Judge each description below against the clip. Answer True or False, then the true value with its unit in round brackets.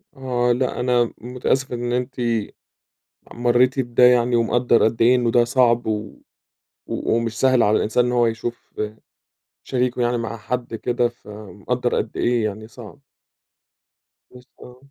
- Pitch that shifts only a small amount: True (1.3 semitones)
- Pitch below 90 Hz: False (120 Hz)